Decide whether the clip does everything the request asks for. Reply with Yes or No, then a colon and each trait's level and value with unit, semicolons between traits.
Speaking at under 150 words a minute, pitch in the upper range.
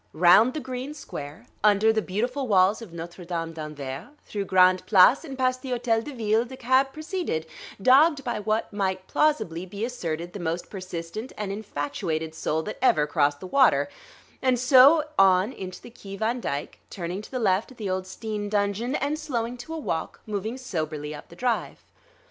No: average, 185 wpm; high, 210 Hz